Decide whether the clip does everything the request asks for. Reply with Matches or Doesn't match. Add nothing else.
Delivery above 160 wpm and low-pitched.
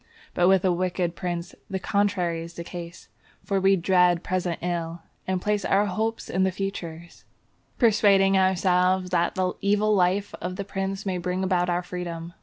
Doesn't match